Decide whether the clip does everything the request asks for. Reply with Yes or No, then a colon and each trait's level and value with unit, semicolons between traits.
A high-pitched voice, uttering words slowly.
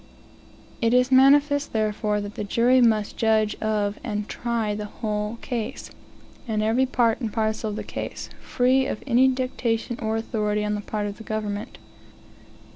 No: high, 220 Hz; average, 165 wpm